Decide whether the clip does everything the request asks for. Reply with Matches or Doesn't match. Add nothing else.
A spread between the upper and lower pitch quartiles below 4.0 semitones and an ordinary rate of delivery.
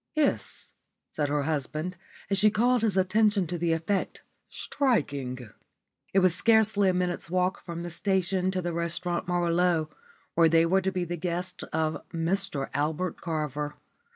Matches